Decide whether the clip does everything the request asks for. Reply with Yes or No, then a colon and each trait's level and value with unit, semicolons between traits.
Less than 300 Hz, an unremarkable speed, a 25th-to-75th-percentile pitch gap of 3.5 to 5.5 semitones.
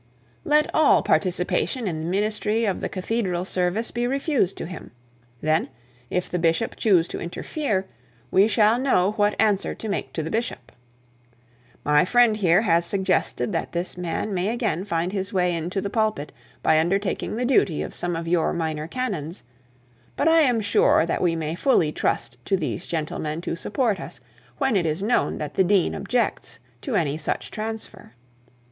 Yes: high, 190 Hz; average, 175 wpm; average, 4.7 semitones